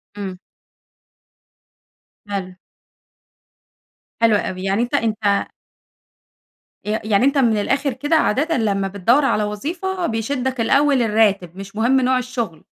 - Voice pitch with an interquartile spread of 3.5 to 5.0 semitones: Yes, average, 4.6 semitones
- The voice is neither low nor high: No, high, 225 Hz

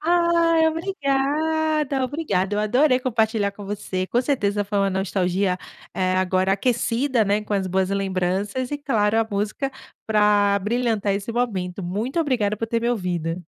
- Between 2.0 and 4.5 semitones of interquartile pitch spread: No, average, 5.1 semitones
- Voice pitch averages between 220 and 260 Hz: No, high, 210 Hz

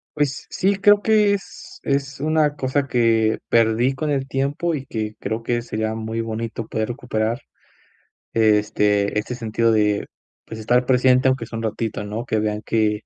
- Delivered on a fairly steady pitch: No, average, 4.0 semitones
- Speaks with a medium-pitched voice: No, low, 115 Hz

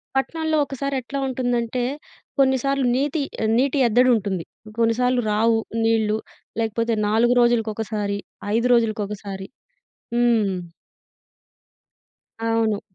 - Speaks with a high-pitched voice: Yes, high, 230 Hz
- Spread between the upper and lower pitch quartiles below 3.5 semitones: Yes, average, 2.9 semitones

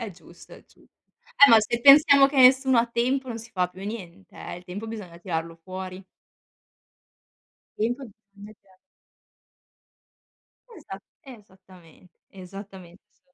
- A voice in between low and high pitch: No, high, 200 Hz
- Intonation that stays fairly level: No, average, 4.5 semitones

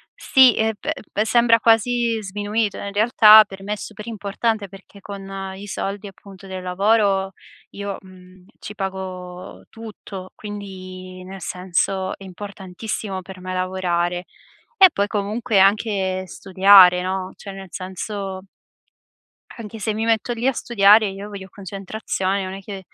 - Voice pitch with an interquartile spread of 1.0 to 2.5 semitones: Yes, narrow, 2.2 semitones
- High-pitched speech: Yes, high, 195 Hz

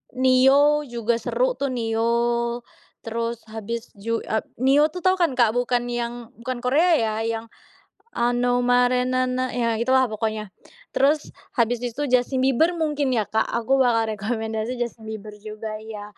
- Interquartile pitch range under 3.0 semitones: Yes, narrow, 2.4 semitones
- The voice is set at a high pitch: Yes, high, 240 Hz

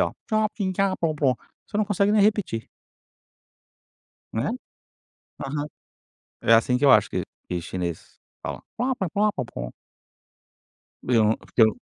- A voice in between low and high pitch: Yes, medium, 145 Hz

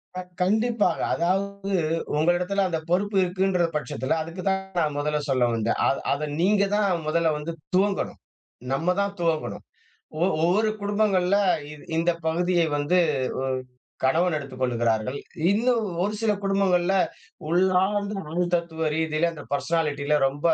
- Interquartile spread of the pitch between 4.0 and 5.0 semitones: Yes, average, 4.3 semitones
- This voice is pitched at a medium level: Yes, medium, 175 Hz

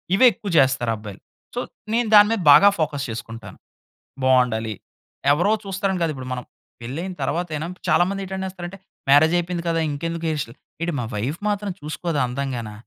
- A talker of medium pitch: Yes, medium, 160 Hz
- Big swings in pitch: Yes, wide, 6.6 semitones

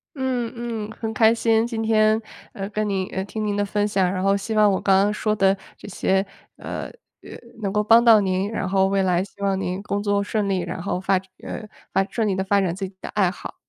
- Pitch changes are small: Yes, narrow, 2.1 semitones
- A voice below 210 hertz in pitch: Yes, high, 200 Hz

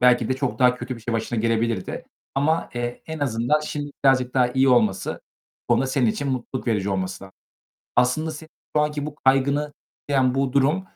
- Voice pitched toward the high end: No, low, 130 Hz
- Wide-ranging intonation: No, average, 3.1 semitones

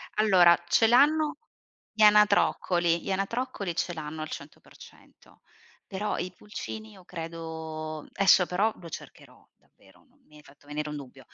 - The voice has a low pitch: No, medium, 175 Hz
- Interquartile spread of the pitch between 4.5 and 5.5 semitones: Yes, average, 5.0 semitones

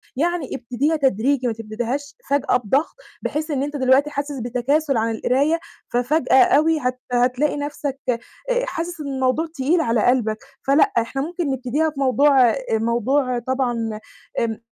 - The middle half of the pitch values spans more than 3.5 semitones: No, average, 3.2 semitones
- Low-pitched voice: No, very high, 265 Hz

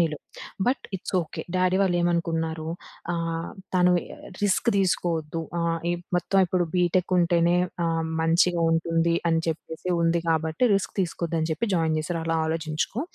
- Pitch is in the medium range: Yes, medium, 170 Hz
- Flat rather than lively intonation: Yes, narrow, 1.4 semitones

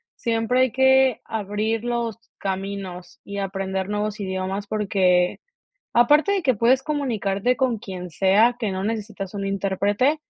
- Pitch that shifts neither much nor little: Yes, average, 3.8 semitones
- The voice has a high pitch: Yes, high, 210 Hz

